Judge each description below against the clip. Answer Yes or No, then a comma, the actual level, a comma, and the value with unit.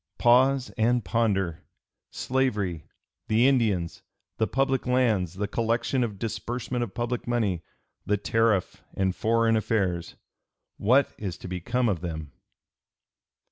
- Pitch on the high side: No, low, 115 Hz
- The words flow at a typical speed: No, slow, 120 wpm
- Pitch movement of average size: Yes, average, 4.3 semitones